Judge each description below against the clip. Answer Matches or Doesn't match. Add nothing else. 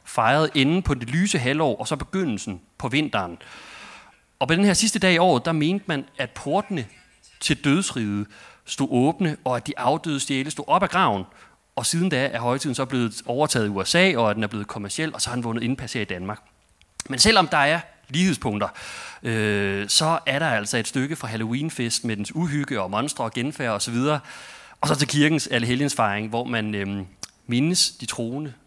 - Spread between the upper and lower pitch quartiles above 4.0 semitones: Matches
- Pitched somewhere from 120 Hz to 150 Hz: Matches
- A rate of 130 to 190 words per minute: Doesn't match